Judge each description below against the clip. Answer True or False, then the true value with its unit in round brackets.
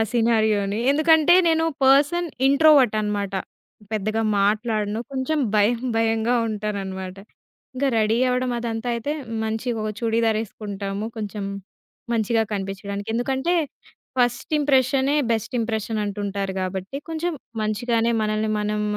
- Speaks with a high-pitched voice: True (225 Hz)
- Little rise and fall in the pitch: False (3.4 semitones)